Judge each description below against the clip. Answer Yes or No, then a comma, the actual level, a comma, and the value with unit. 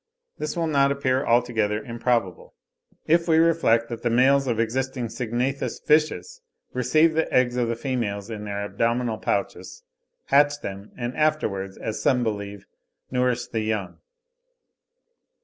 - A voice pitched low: Yes, low, 120 Hz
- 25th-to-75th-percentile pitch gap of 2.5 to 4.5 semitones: Yes, average, 4.0 semitones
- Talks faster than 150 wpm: No, average, 145 wpm